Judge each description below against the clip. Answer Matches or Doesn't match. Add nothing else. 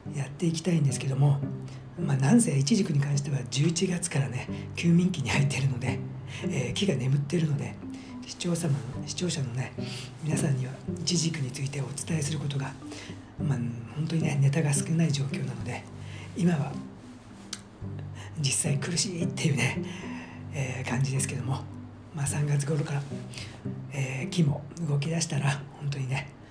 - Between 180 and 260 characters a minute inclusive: Doesn't match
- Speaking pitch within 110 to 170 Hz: Matches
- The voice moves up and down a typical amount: Matches